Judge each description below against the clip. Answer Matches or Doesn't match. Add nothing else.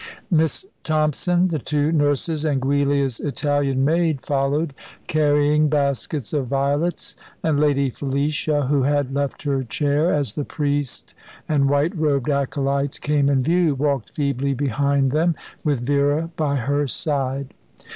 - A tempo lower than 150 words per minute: Matches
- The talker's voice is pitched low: Doesn't match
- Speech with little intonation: Matches